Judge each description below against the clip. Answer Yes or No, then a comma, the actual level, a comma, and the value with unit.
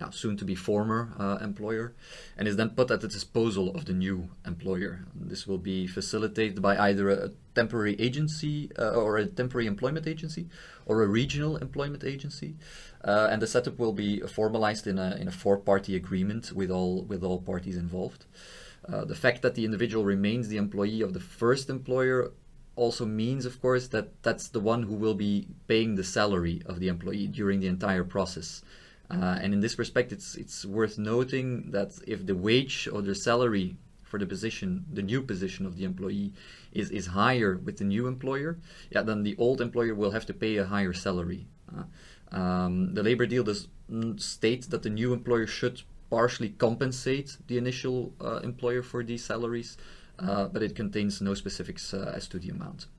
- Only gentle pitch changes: No, average, 3.8 semitones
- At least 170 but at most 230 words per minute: Yes, average, 190 wpm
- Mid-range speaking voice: No, low, 110 Hz